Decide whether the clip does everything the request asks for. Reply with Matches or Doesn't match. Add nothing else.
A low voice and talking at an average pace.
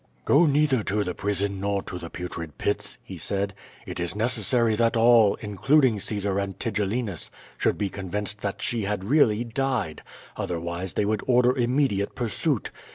Matches